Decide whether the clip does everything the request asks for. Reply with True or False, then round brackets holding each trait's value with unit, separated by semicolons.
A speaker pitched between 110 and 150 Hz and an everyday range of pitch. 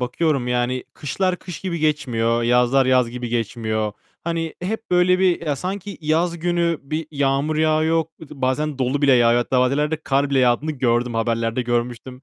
True (135 Hz; 4.7 semitones)